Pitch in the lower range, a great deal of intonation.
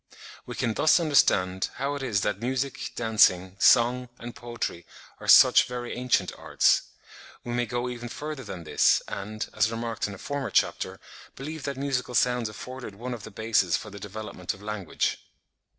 No: low, 120 Hz; average, 3.4 semitones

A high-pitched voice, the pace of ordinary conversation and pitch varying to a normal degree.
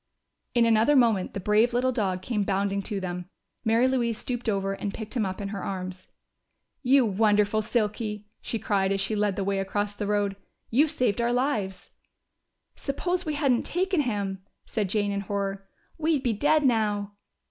Yes: high, 210 Hz; average, 180 wpm; average, 3.6 semitones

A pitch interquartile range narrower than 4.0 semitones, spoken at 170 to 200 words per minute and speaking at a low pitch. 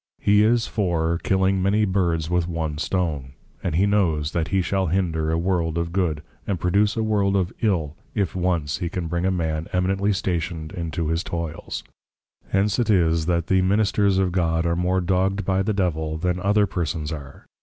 Yes: average, 2.9 semitones; average, 185 wpm; very low, 90 Hz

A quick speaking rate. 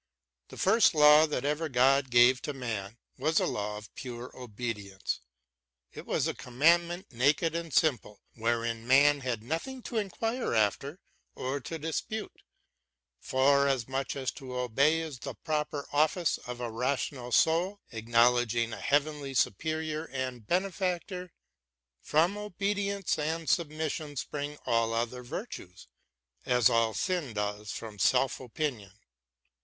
No: slow, 135 wpm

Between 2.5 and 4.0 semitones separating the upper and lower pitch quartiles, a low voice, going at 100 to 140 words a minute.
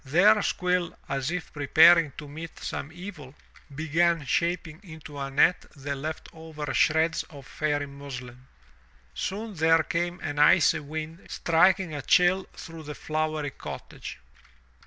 No: average, 2.9 semitones; medium, 160 Hz; slow, 135 wpm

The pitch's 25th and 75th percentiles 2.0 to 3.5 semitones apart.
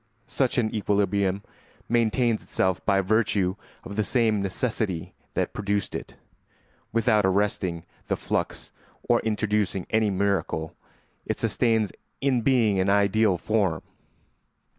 Yes: narrow, 2.4 semitones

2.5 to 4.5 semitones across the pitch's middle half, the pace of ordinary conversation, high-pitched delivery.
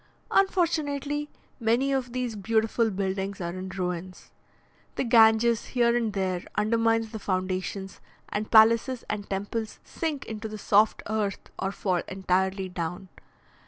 No: average, 3.5 semitones; slow, 130 wpm; high, 215 Hz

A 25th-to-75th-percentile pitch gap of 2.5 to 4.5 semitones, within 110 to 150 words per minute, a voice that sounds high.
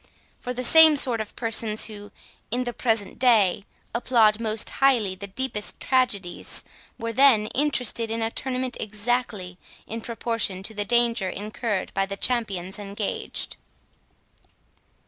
Yes: average, 3.2 semitones; slow, 135 wpm; high, 225 Hz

